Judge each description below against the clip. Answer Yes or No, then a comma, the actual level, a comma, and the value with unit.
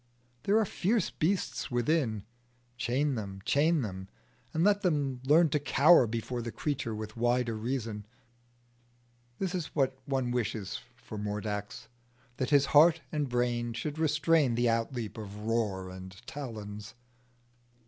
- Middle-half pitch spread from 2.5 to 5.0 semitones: No, wide, 5.5 semitones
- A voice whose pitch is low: Yes, low, 125 Hz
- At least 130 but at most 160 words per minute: Yes, average, 140 wpm